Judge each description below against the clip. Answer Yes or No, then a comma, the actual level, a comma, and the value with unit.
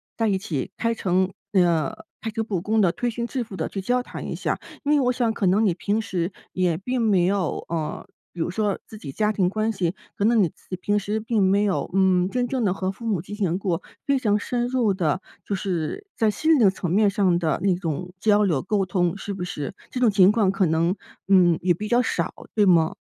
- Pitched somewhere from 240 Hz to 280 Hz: No, high, 195 Hz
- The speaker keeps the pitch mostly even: No, average, 3.5 semitones